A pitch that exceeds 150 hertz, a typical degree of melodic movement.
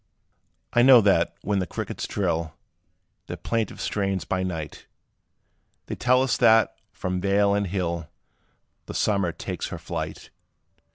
No: low, 100 Hz; average, 3.5 semitones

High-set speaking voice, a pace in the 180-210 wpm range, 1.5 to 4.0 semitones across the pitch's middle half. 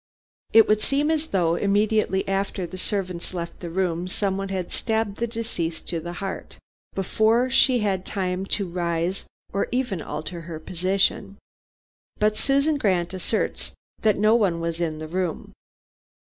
No: high, 195 Hz; average, 155 wpm; average, 3.7 semitones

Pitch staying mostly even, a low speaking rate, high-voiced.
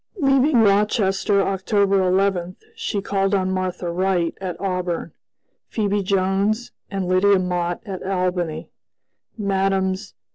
Yes: narrow, 1.5 semitones; slow, 110 wpm; high, 195 Hz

